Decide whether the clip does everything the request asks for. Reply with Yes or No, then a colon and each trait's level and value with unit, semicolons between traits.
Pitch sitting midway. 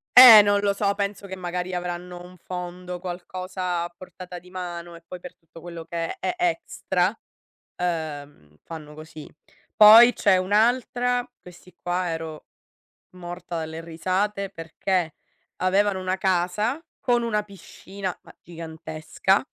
Yes: medium, 180 Hz